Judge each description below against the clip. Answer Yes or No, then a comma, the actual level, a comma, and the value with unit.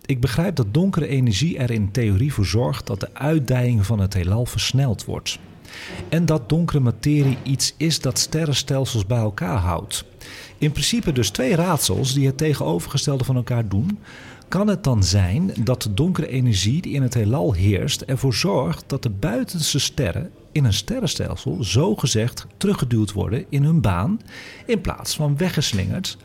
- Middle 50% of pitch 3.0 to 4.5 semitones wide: No, average, 5.3 semitones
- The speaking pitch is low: Yes, low, 130 Hz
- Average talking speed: Yes, average, 165 wpm